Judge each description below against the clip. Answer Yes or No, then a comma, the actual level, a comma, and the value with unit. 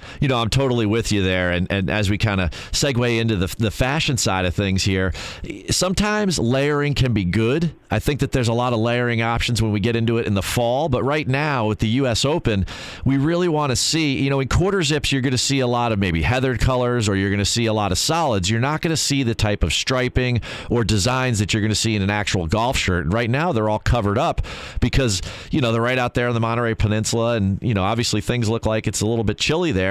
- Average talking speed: No, fast, 265 wpm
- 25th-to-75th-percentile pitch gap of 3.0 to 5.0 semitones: Yes, average, 3.9 semitones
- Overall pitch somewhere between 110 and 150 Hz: Yes, low, 115 Hz